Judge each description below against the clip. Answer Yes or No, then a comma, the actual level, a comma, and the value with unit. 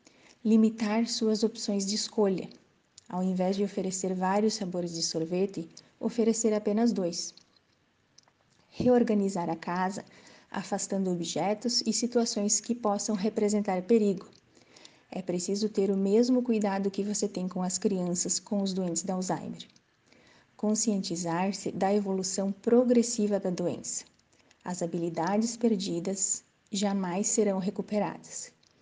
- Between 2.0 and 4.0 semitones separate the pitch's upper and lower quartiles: Yes, average, 2.8 semitones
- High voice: Yes, high, 200 Hz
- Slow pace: Yes, slow, 115 wpm